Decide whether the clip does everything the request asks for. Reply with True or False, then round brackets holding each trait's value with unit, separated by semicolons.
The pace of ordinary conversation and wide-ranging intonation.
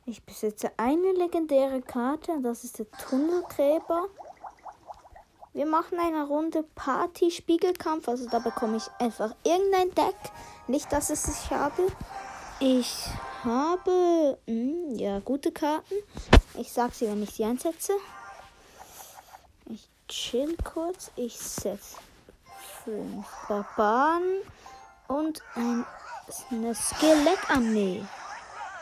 False (100 wpm; 6.4 semitones)